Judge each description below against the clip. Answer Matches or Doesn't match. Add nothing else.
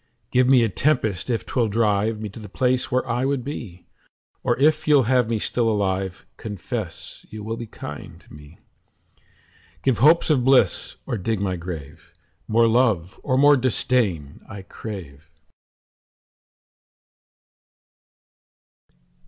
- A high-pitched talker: Doesn't match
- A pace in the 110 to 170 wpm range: Matches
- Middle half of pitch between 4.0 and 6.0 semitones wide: Matches